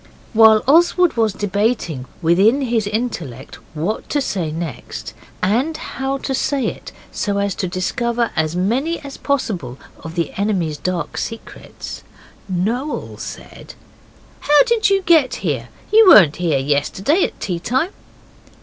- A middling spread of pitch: No, wide, 7.7 semitones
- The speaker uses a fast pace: No, average, 140 wpm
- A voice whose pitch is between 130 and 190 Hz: No, high, 215 Hz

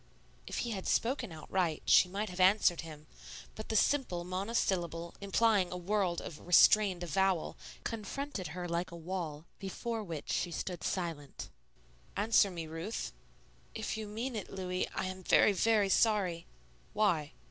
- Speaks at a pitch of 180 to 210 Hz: Yes, medium, 185 Hz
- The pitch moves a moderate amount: Yes, average, 3.7 semitones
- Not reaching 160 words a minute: Yes, average, 150 wpm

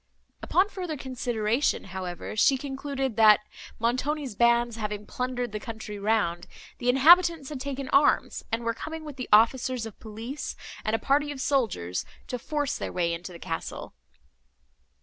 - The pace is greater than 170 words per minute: No, average, 155 wpm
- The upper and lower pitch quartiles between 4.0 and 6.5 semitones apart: Yes, average, 4.6 semitones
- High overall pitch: Yes, high, 240 Hz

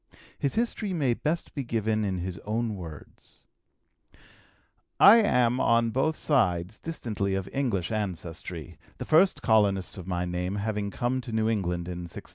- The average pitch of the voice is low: Yes, low, 110 Hz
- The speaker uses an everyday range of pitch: No, wide, 5.7 semitones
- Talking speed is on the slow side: No, average, 155 wpm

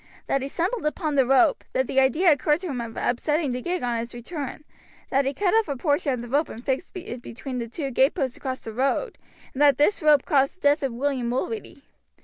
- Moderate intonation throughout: Yes, average, 3.5 semitones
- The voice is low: No, very high, 275 Hz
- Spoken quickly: Yes, fast, 235 wpm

